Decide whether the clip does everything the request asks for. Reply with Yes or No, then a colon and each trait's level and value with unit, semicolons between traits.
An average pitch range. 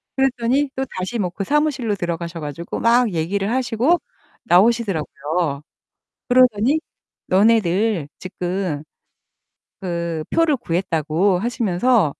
No: wide, 6.0 semitones